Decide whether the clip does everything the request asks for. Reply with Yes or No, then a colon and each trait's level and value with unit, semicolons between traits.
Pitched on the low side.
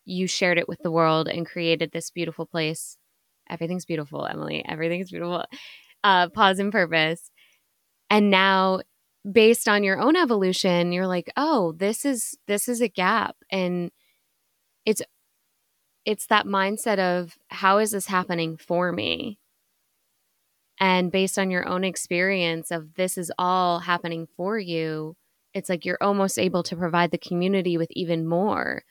No: medium, 180 Hz